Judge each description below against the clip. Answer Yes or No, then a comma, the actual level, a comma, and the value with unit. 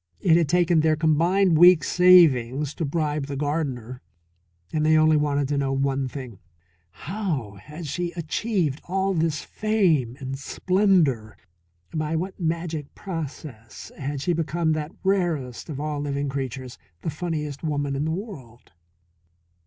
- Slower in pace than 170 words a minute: Yes, average, 145 wpm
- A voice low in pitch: No, medium, 155 Hz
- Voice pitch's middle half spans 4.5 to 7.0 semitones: No, average, 3.8 semitones